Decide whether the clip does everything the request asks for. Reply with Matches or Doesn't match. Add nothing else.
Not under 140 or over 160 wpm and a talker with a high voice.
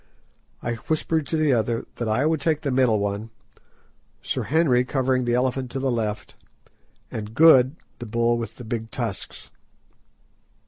Doesn't match